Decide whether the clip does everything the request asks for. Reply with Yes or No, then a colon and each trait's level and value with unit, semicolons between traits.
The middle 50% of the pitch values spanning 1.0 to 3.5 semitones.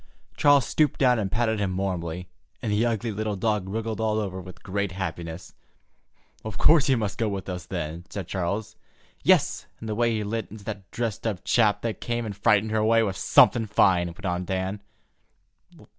Yes: average, 3.0 semitones